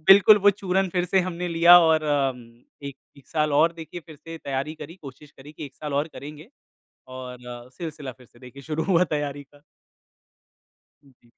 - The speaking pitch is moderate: Yes, medium, 150 Hz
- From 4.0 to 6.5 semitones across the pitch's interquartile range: No, average, 3.6 semitones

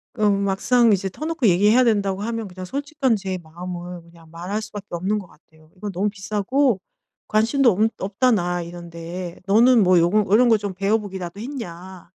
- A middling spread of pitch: Yes, average, 3.8 semitones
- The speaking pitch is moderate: No, high, 195 Hz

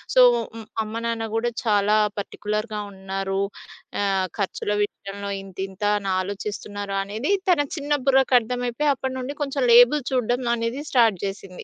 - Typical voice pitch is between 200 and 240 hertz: Yes, high, 215 Hz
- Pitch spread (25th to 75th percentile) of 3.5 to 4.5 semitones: Yes, average, 4.0 semitones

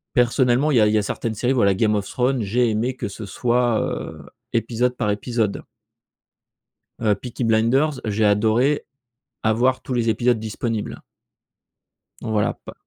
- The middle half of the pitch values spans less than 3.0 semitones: Yes, narrow, 2.6 semitones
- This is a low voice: Yes, low, 115 Hz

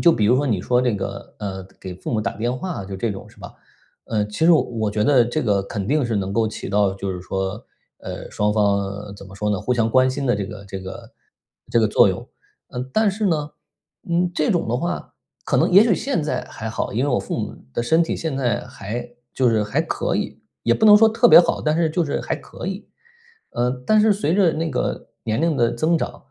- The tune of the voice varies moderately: No, wide, 7.6 semitones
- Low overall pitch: Yes, low, 120 Hz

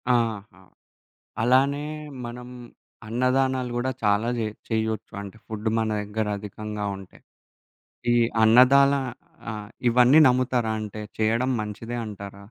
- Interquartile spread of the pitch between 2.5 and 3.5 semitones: Yes, average, 2.9 semitones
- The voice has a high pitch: No, low, 115 Hz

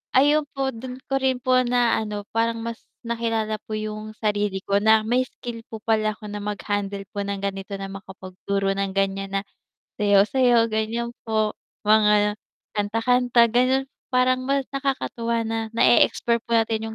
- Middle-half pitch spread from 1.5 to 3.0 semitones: Yes, average, 2.7 semitones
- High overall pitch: Yes, high, 220 Hz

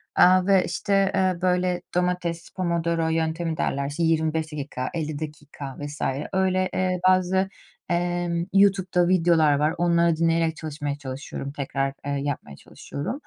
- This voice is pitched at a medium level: Yes, medium, 170 Hz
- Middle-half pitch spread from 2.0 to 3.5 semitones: Yes, average, 3.2 semitones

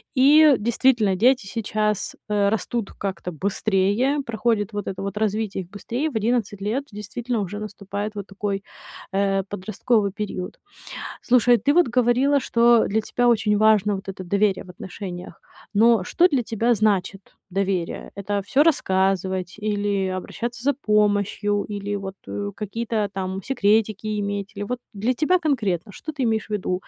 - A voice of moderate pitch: No, high, 210 Hz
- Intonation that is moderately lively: Yes, average, 3.1 semitones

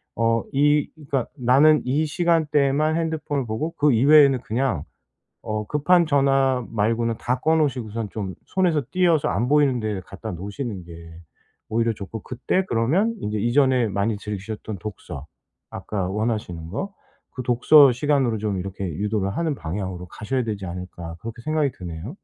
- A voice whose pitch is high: No, low, 120 Hz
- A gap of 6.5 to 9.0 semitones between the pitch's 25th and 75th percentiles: No, wide, 5.9 semitones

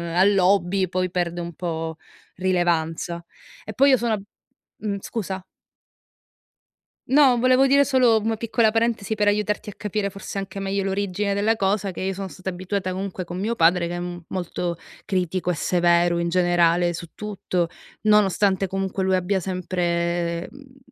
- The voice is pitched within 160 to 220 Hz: Yes, high, 190 Hz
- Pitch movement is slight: No, average, 3.0 semitones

